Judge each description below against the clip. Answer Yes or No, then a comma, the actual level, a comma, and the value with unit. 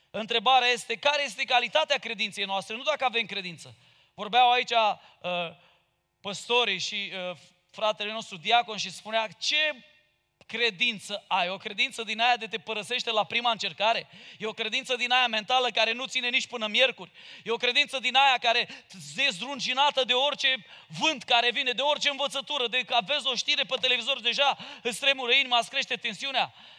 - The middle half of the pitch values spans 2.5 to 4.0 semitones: Yes, average, 3.4 semitones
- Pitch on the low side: No, high, 240 Hz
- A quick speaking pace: Yes, fast, 175 wpm